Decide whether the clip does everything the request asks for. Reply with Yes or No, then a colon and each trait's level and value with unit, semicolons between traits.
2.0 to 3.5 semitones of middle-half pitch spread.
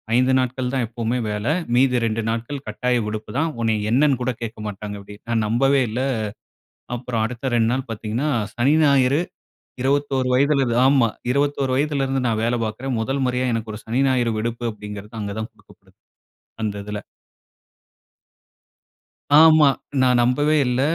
Yes: average, 3.2 semitones